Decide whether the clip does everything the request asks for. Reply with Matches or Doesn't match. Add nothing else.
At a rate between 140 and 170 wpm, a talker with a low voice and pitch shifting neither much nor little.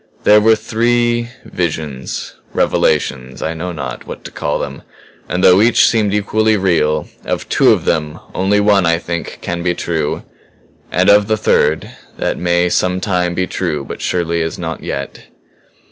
Matches